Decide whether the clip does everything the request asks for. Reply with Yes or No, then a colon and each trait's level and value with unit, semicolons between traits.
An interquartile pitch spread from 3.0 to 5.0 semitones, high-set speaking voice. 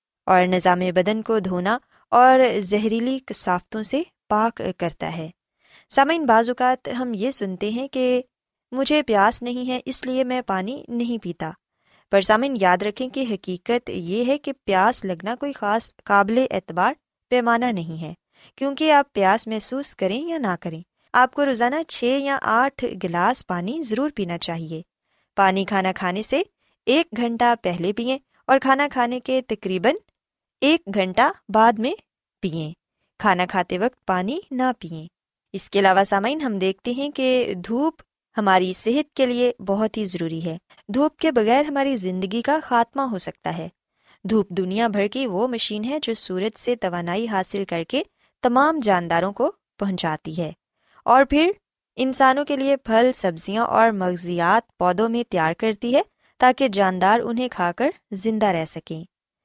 No: wide, 5.4 semitones; high, 225 Hz